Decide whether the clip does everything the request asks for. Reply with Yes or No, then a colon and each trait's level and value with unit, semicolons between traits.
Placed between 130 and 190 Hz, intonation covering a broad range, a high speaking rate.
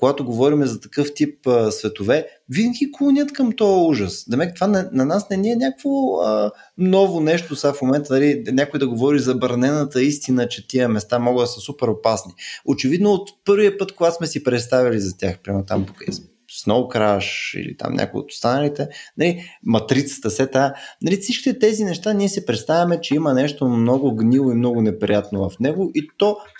Yes: medium, 140 Hz; wide, 7.9 semitones; fast, 185 wpm